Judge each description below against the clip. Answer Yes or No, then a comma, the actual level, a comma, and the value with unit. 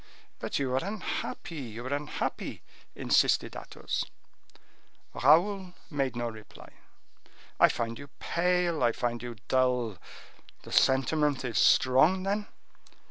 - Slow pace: Yes, slow, 120 wpm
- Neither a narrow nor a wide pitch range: No, wide, 5.8 semitones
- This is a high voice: No, low, 135 Hz